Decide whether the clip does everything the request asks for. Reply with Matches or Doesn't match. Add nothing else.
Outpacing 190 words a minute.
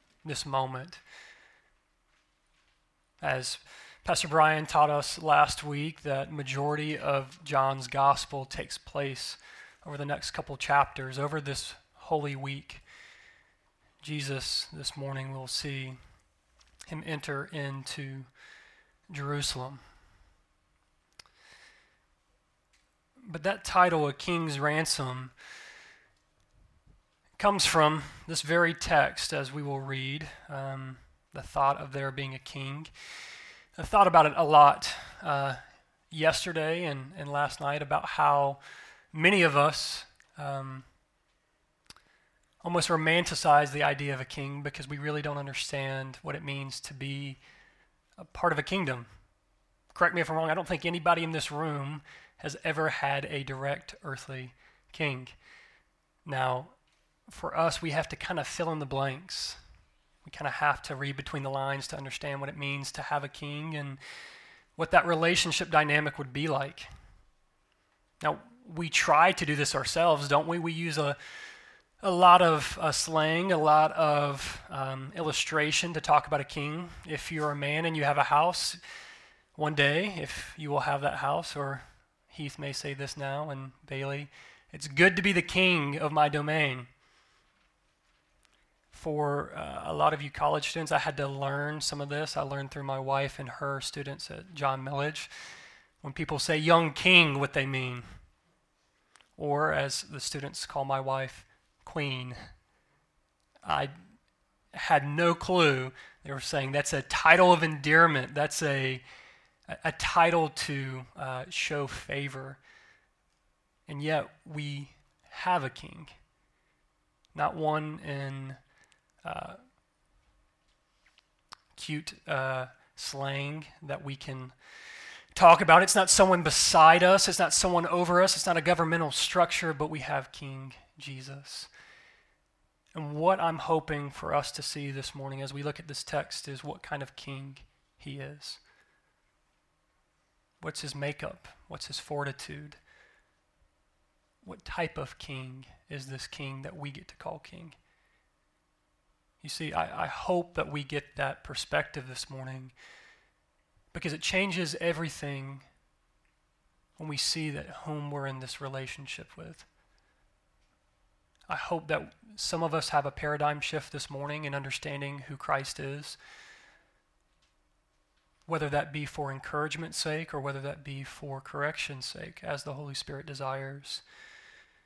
Doesn't match